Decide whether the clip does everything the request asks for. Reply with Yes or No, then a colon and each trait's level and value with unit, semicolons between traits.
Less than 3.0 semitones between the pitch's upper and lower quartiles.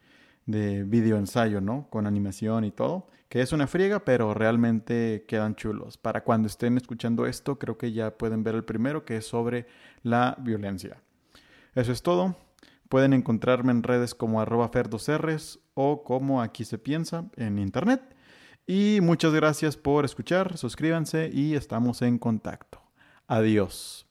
No: average, 4.7 semitones